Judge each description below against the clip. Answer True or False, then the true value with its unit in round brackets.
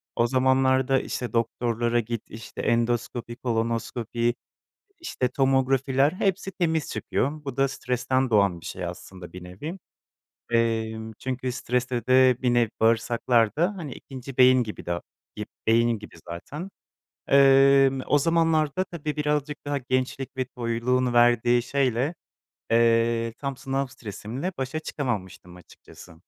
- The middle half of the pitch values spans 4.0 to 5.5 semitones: False (2.9 semitones)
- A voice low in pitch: True (125 Hz)